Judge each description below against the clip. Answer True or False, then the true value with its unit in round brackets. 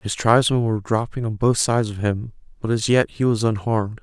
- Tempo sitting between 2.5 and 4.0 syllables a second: False (6.0 syllables/s)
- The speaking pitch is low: True (110 Hz)